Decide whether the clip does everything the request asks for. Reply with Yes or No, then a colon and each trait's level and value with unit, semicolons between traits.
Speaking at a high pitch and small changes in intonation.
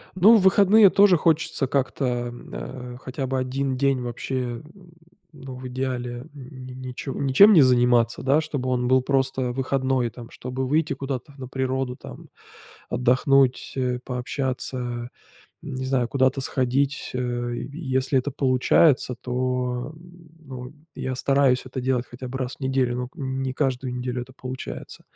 No: low, 130 Hz; narrow, 1.5 semitones